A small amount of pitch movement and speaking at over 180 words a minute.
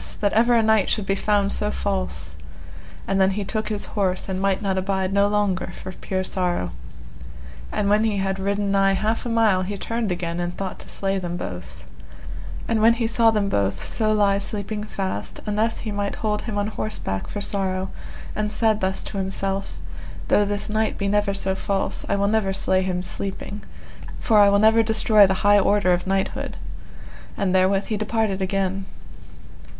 Yes: narrow, 1.9 semitones; average, 190 wpm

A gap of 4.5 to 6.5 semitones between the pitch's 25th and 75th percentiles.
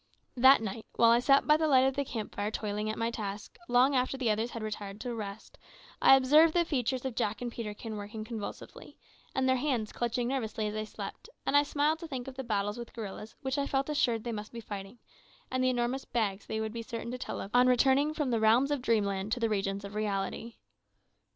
No: average, 3.6 semitones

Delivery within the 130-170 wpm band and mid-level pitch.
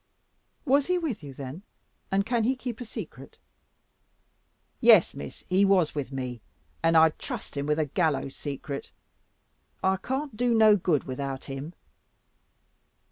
Yes: average, 145 wpm; medium, 165 Hz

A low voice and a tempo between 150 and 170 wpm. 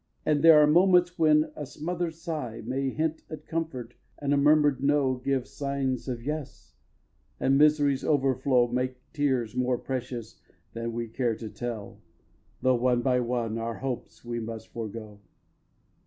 Yes: low, 130 Hz; average, 155 wpm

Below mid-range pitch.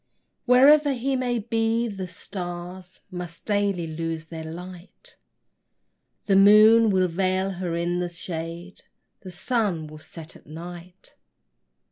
No: medium, 185 Hz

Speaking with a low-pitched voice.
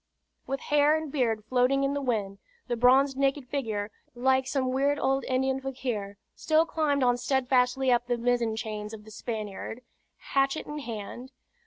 No: very high, 255 Hz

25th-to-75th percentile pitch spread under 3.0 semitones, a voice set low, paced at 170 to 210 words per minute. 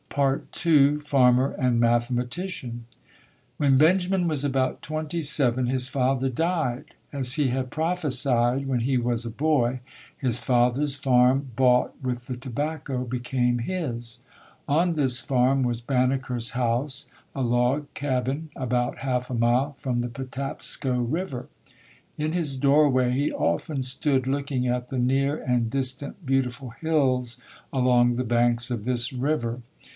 No: narrow, 2.5 semitones; low, 130 Hz; slow, 135 wpm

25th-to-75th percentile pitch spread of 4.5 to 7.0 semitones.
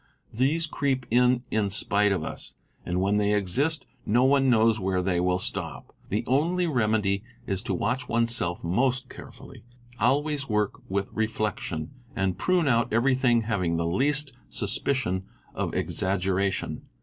Yes: wide, 5.4 semitones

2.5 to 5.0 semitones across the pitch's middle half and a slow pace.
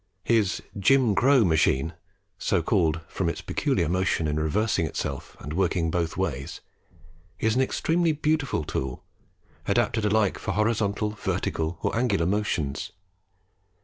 No: wide, 5.5 semitones; slow, 130 wpm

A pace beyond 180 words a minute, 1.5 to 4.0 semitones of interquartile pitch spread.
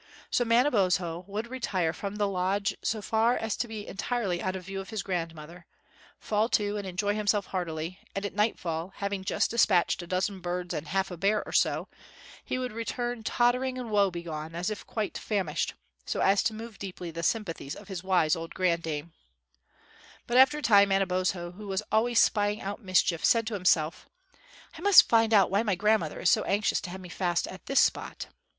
Yes: average, 195 wpm; average, 3.5 semitones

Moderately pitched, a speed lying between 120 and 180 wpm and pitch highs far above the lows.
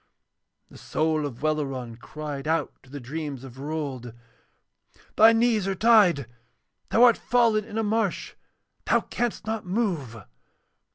Yes: medium, 160 Hz; average, 145 wpm; wide, 8.1 semitones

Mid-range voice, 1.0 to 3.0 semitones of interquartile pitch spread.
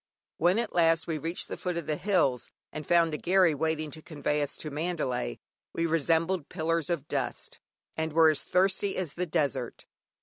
Yes: medium, 160 Hz; narrow, 2.4 semitones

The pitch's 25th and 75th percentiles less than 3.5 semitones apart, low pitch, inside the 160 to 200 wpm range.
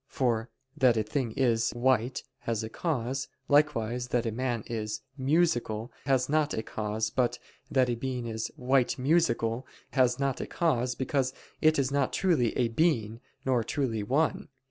Yes: average, 3.0 semitones; low, 125 Hz; average, 165 wpm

